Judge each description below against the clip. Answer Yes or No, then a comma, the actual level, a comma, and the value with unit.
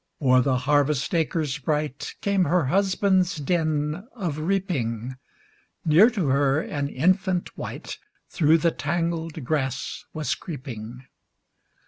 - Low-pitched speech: No, medium, 155 Hz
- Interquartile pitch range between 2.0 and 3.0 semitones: No, average, 4.4 semitones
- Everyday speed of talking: No, slow, 115 wpm